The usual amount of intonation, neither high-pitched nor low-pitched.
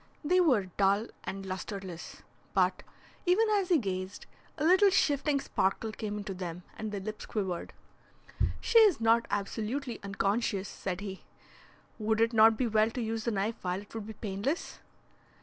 No: average, 4.2 semitones; high, 215 Hz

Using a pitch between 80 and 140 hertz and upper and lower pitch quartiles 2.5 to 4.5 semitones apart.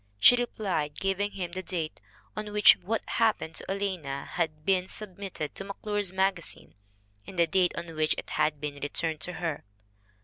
No: medium, 180 Hz; average, 4.2 semitones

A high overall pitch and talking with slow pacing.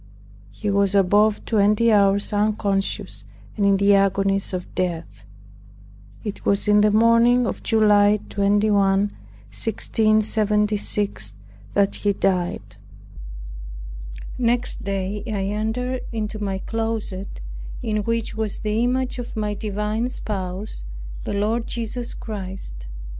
Yes: high, 210 Hz; slow, 115 wpm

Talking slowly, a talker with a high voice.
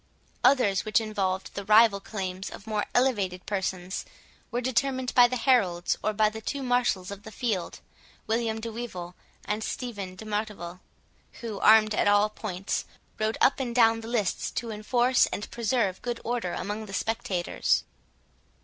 No: average, 160 wpm; high, 215 Hz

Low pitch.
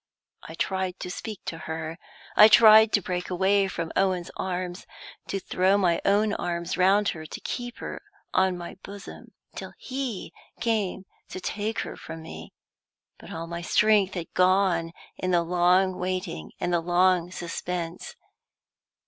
No: medium, 185 Hz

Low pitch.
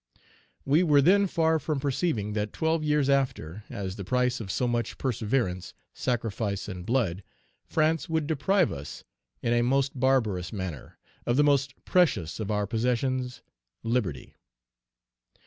Yes: low, 125 Hz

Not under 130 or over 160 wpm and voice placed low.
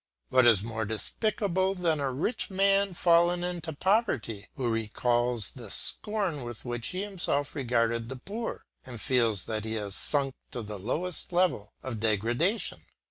Yes: average, 155 wpm; low, 130 Hz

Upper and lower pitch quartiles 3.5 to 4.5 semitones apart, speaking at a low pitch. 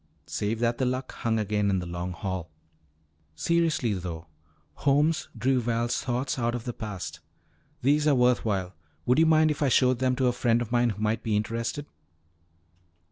Yes: average, 3.8 semitones; low, 120 Hz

